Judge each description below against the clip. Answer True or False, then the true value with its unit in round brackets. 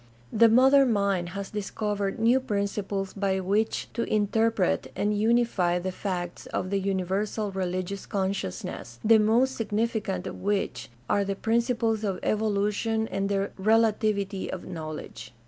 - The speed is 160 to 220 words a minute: False (140 wpm)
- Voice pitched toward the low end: False (200 Hz)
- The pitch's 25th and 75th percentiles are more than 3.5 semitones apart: False (2.5 semitones)